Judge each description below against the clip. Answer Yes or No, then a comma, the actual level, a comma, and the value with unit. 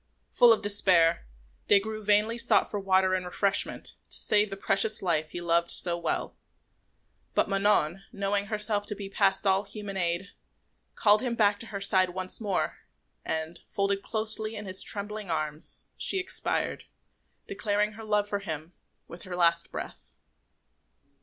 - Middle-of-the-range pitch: No, high, 200 Hz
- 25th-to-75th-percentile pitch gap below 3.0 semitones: Yes, narrow, 2.6 semitones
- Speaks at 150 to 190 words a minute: Yes, average, 160 wpm